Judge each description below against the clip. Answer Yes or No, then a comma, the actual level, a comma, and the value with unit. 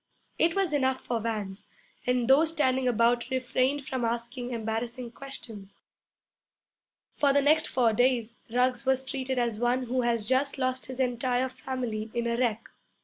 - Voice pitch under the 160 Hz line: No, very high, 250 Hz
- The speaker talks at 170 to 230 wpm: No, average, 155 wpm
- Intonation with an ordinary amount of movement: No, narrow, 2.0 semitones